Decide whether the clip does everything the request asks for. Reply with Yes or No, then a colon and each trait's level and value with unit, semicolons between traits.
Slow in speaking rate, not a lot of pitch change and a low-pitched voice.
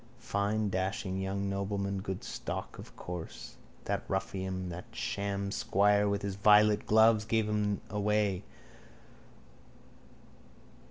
Yes: slow, 110 wpm; narrow, 1.5 semitones; low, 100 Hz